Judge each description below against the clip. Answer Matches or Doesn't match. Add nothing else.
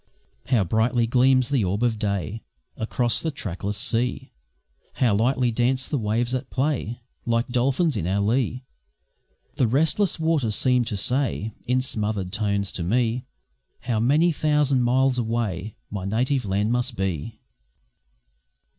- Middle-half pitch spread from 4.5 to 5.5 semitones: Doesn't match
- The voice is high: Doesn't match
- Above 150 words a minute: Doesn't match